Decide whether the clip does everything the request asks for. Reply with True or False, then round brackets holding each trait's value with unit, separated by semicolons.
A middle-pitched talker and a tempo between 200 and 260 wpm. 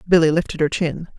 True (160 Hz; 205 wpm)